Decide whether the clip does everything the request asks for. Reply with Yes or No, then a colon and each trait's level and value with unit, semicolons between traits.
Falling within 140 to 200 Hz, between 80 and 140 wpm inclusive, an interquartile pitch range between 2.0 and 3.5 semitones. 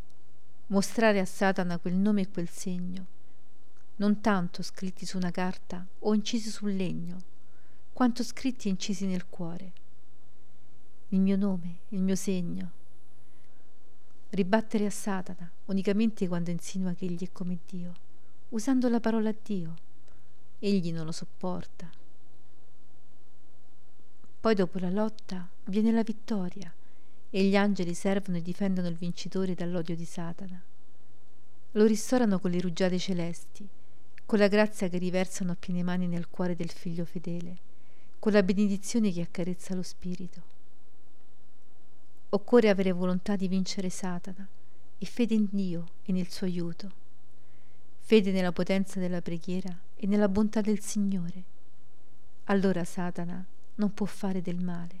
Yes: medium, 185 Hz; average, 135 wpm; narrow, 2.4 semitones